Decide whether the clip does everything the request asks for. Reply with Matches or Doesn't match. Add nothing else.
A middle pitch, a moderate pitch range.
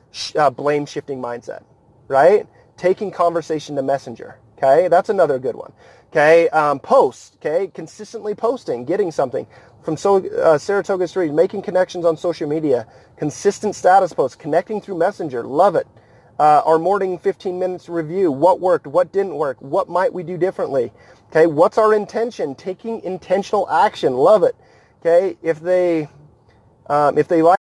Matches